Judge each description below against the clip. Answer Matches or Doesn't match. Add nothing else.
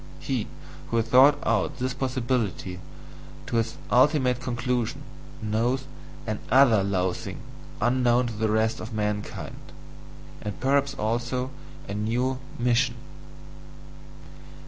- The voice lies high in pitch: Doesn't match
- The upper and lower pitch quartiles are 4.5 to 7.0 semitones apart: Doesn't match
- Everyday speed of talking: Doesn't match